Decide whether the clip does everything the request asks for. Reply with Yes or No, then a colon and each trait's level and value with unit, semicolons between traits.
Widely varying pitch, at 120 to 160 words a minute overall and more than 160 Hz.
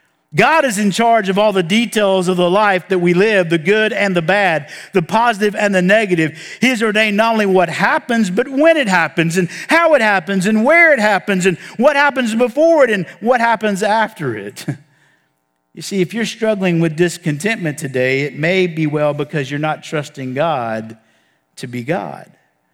No: wide, 6.1 semitones; average, 195 wpm; high, 190 Hz